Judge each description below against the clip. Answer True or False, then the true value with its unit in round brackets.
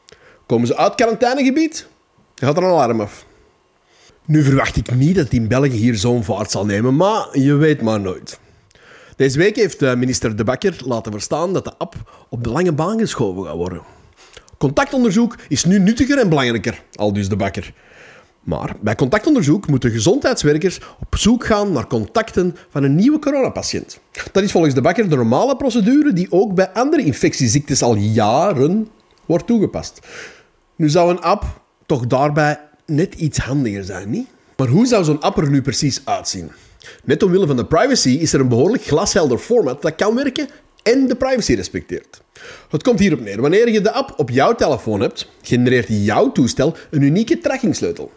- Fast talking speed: False (175 wpm)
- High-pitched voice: False (150 Hz)